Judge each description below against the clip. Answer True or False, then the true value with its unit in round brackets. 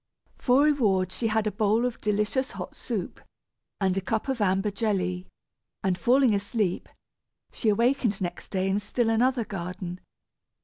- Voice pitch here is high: True (210 Hz)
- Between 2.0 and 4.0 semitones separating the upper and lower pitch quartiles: True (3.7 semitones)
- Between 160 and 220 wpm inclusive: False (150 wpm)